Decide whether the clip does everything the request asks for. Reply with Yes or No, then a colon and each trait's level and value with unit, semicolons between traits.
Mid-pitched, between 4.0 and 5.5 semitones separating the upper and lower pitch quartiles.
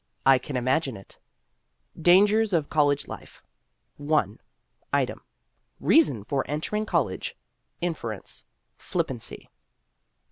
Yes: medium, 150 Hz; average, 5.2 semitones